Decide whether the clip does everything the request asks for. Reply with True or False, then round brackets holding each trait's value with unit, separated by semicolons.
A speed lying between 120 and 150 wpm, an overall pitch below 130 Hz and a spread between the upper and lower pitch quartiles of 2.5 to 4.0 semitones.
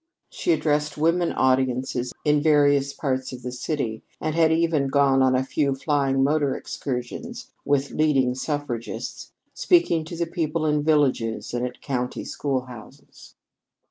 False (140 wpm; 140 Hz; 3.1 semitones)